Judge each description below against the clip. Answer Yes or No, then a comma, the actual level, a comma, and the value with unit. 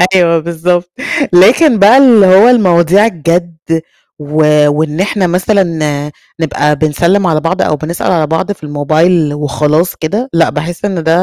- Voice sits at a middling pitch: Yes, medium, 170 Hz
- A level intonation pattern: No, average, 3.5 semitones